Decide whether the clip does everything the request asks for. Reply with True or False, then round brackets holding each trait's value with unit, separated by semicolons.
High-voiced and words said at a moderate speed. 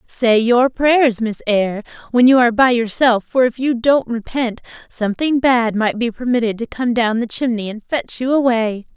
True (240 Hz; 195 wpm)